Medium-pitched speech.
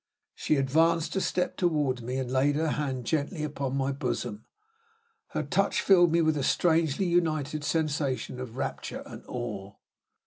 Yes: medium, 145 Hz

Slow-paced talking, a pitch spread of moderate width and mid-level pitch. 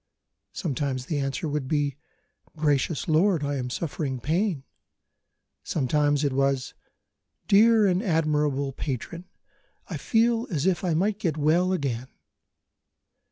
Yes: slow, 120 wpm; average, 4.5 semitones; medium, 150 Hz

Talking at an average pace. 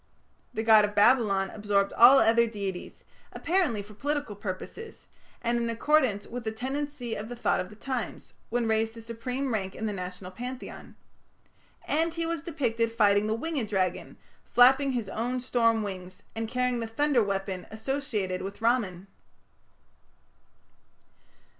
Yes: average, 150 wpm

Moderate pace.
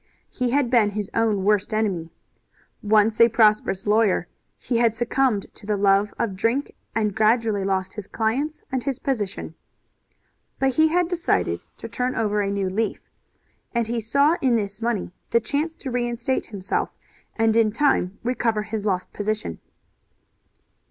Yes: average, 160 wpm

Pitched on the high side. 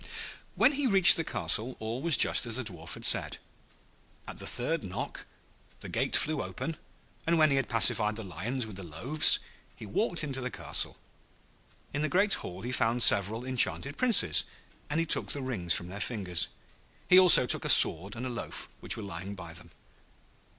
No: low, 120 Hz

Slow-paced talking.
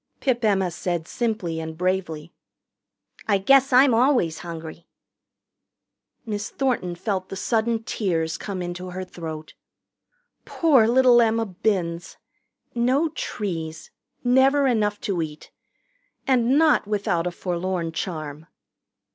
Yes: slow, 115 wpm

